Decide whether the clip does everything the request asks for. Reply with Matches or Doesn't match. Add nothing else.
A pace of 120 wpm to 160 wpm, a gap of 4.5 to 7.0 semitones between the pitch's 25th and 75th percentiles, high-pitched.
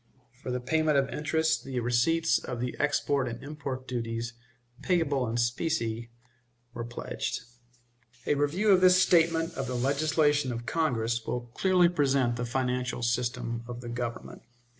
Doesn't match